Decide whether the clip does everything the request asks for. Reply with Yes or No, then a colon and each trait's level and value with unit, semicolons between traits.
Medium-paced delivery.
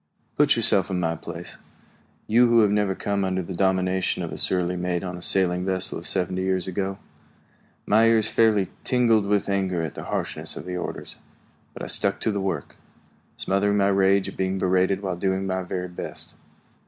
Yes: average, 190 wpm